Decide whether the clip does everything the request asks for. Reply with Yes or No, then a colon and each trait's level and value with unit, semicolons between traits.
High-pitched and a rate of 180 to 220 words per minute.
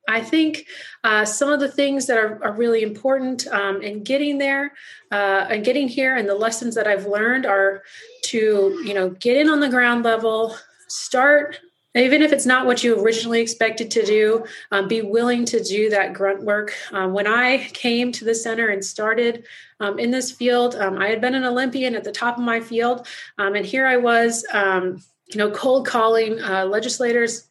Yes: high, 230 Hz; average, 200 wpm